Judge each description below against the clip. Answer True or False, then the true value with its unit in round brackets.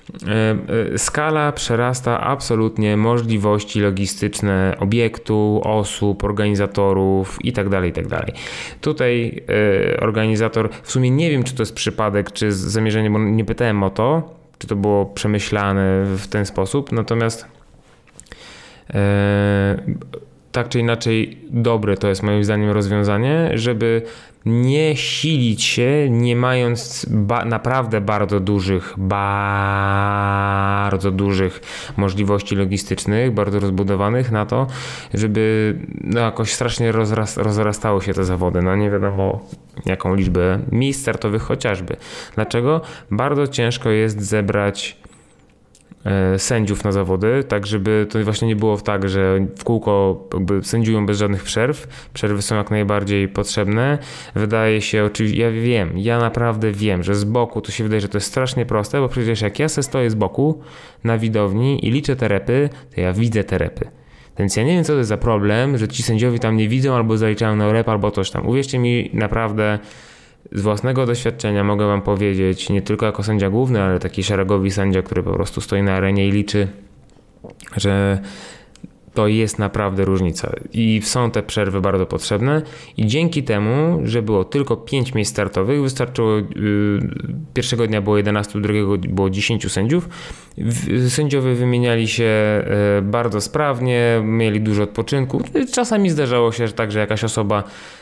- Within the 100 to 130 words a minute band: False (145 wpm)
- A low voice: True (110 Hz)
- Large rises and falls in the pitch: False (2.9 semitones)